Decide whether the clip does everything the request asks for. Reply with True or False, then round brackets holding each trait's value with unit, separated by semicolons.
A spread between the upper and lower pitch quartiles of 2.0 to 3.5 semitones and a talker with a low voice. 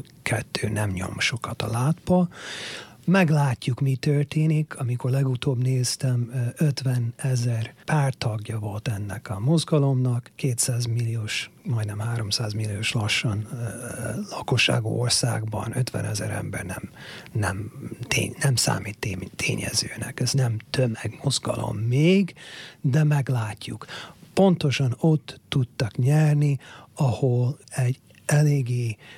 False (3.9 semitones; 125 Hz)